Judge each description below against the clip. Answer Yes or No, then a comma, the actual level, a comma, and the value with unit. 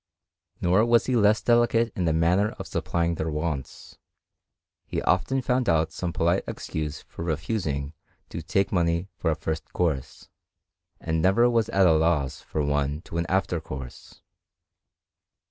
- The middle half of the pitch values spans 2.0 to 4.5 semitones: Yes, average, 4.1 semitones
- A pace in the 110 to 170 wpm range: Yes, average, 155 wpm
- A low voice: Yes, very low, 85 Hz